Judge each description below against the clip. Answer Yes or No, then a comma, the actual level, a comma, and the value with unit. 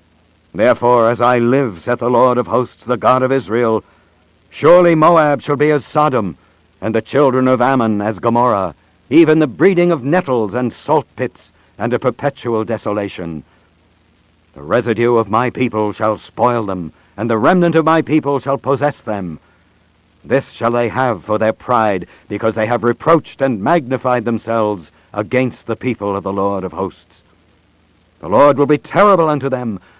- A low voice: Yes, low, 115 Hz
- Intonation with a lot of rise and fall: Yes, wide, 6.0 semitones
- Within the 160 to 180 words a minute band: Yes, average, 170 wpm